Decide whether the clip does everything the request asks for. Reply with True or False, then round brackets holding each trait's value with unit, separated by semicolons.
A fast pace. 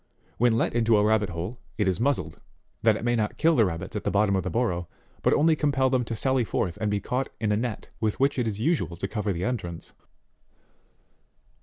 True (225 wpm)